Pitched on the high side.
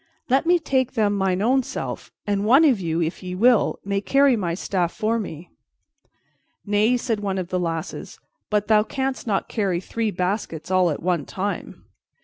Yes: high, 205 Hz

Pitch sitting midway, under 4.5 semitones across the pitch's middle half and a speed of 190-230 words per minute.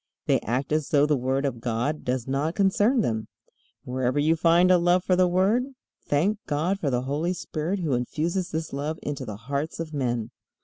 No: medium, 150 Hz; average, 5.2 semitones; average, 200 wpm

